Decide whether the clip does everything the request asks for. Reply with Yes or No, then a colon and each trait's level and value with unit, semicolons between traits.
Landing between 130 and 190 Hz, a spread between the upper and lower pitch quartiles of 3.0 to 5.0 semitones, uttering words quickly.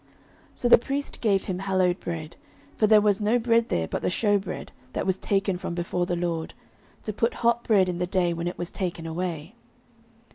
Yes: medium, 185 Hz; average, 3.5 semitones; fast, 210 wpm